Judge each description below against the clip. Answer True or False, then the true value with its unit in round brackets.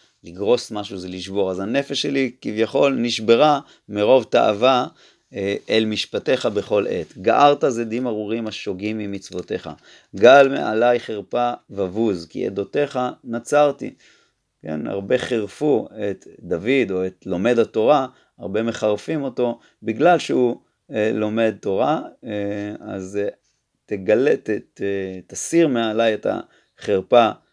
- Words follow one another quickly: False (120 wpm)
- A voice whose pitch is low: True (110 Hz)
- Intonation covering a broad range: False (3.5 semitones)